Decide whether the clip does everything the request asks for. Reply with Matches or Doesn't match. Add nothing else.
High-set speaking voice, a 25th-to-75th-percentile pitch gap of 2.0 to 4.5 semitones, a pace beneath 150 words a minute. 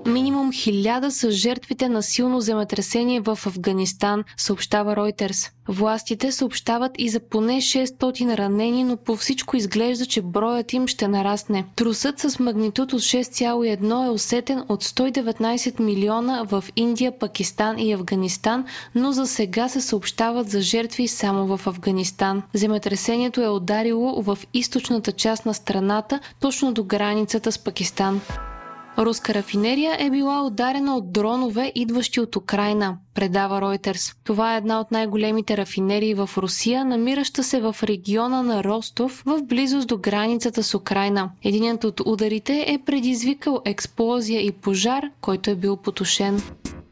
Matches